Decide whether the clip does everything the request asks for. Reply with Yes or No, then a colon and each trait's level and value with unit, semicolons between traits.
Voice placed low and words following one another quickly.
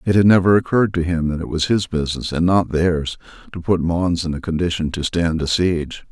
Yes: very low, 85 Hz; fast, 235 wpm